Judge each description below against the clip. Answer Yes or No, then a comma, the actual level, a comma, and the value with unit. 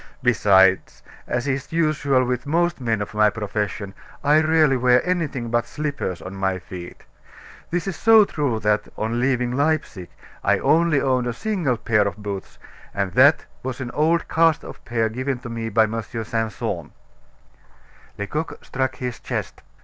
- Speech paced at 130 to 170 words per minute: Yes, average, 155 wpm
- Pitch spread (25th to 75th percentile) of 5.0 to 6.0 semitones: Yes, wide, 5.5 semitones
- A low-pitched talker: Yes, low, 125 Hz